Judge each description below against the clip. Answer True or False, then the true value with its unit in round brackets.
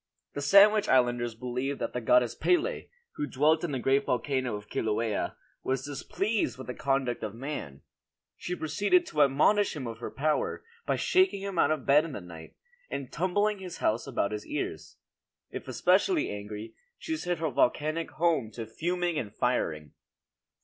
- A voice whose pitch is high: False (140 Hz)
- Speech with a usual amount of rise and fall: False (6.7 semitones)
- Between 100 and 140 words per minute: False (170 wpm)